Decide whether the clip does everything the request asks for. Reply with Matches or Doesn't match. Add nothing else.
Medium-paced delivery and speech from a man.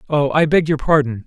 Doesn't match